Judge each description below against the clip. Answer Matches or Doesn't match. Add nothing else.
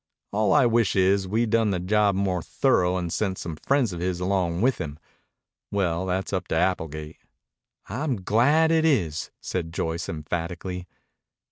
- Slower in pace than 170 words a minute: Matches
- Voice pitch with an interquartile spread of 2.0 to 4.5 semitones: Matches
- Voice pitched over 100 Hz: Doesn't match